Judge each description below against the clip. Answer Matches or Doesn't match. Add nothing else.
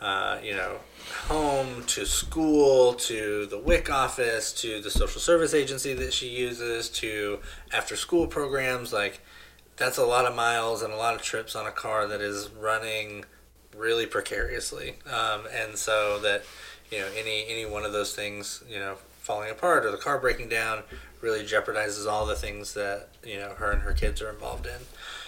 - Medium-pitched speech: Doesn't match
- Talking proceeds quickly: Doesn't match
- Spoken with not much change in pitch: Doesn't match